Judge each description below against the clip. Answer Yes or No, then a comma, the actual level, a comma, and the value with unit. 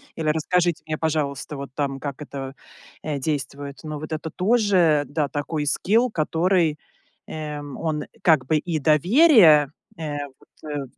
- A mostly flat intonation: Yes, narrow, 2.3 semitones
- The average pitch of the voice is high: No, medium, 155 Hz